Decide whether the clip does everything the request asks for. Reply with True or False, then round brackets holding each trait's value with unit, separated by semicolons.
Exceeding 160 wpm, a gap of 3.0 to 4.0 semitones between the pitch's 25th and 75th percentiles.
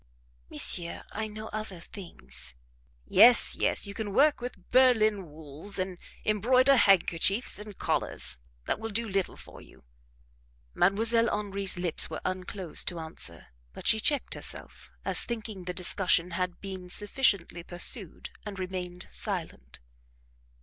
False (135 wpm; 3.7 semitones)